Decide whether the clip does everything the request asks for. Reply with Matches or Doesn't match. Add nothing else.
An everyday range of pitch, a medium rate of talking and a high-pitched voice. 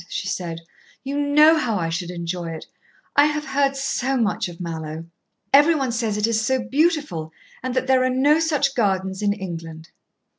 Doesn't match